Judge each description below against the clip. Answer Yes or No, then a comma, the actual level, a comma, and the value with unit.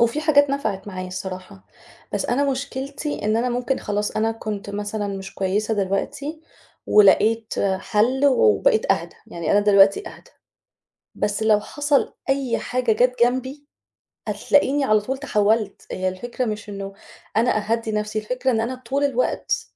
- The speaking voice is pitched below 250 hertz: Yes, high, 225 Hz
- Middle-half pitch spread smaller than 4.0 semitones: No, average, 4.4 semitones